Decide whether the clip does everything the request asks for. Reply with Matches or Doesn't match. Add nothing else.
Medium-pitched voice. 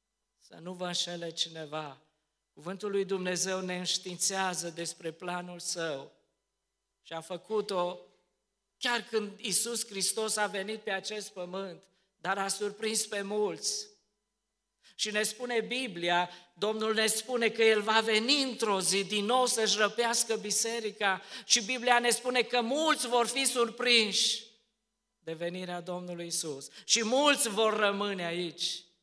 Doesn't match